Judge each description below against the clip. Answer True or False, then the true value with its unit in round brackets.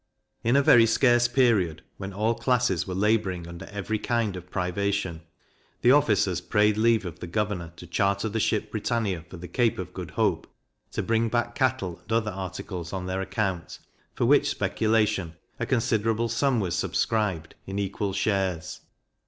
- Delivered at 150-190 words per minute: True (170 wpm)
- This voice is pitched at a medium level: False (105 Hz)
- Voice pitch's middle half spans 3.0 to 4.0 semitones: True (3.7 semitones)